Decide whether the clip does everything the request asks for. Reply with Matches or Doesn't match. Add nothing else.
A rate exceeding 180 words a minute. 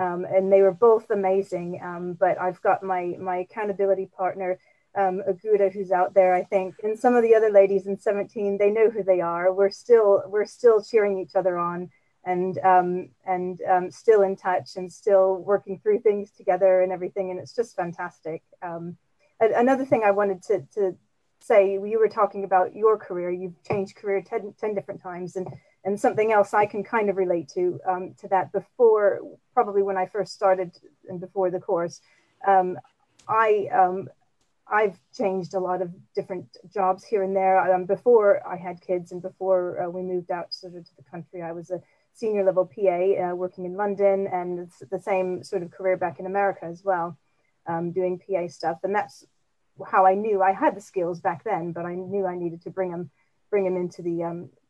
Matches